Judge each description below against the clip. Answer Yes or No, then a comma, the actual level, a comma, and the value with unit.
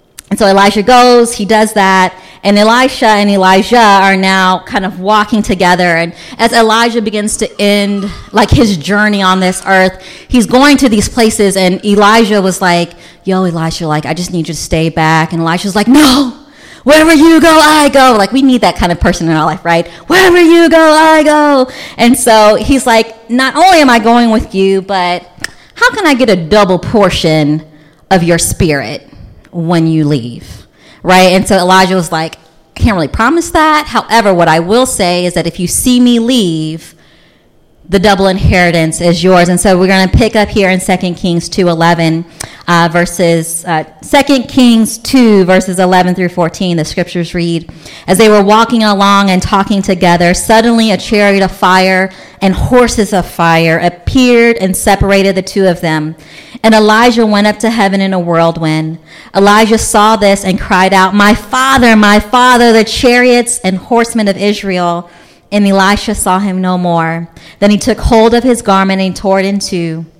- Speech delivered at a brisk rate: No, average, 185 wpm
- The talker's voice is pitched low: No, high, 195 Hz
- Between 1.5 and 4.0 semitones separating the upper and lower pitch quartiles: No, average, 4.4 semitones